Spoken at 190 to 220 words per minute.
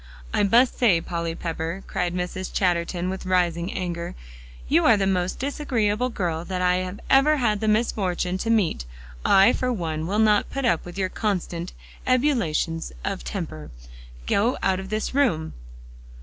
No: average, 160 wpm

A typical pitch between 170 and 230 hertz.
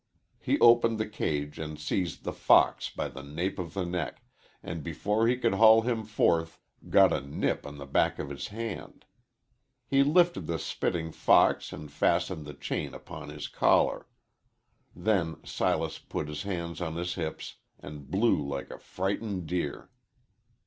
No: very low, 85 Hz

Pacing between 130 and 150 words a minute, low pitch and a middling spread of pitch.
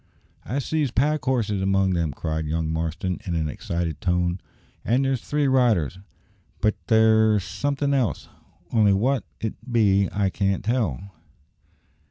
No: average, 140 wpm; low, 100 Hz; wide, 6.0 semitones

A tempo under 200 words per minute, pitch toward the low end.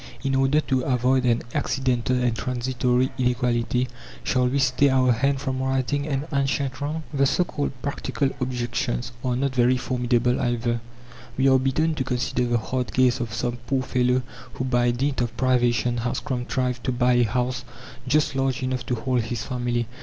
Yes: average, 175 wpm; low, 125 Hz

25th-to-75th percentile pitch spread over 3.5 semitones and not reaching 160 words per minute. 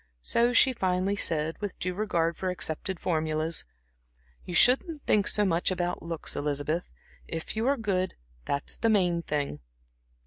Yes: average, 4.2 semitones; average, 150 wpm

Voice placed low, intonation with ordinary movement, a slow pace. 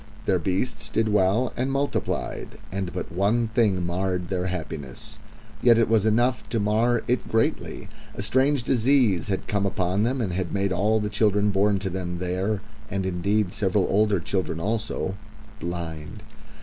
No: low, 100 Hz; average, 3.4 semitones; average, 160 wpm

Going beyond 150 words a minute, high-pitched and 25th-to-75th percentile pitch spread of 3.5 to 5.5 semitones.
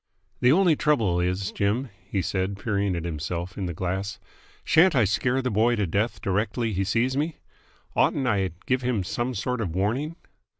No: average, 185 wpm; low, 105 Hz; average, 5.0 semitones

